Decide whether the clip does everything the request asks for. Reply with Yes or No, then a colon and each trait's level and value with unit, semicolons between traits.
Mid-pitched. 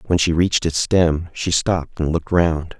No: very low, 85 Hz